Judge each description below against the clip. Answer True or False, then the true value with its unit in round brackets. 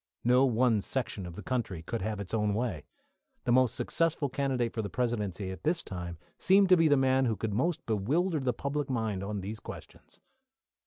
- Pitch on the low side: True (120 Hz)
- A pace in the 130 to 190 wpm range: False (200 wpm)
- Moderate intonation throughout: True (4.7 semitones)